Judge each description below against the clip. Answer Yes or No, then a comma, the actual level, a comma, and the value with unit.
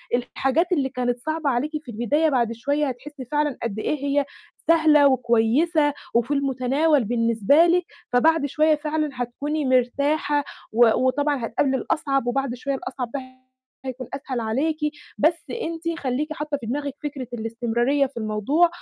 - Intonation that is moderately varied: Yes, average, 3.7 semitones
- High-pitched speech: Yes, very high, 275 Hz